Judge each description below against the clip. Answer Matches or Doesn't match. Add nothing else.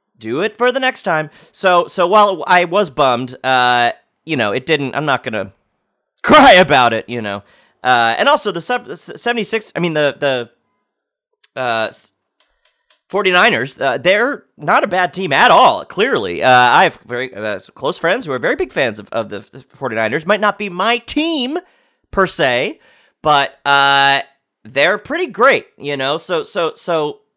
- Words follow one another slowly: Doesn't match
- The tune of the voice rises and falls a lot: Matches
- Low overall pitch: Doesn't match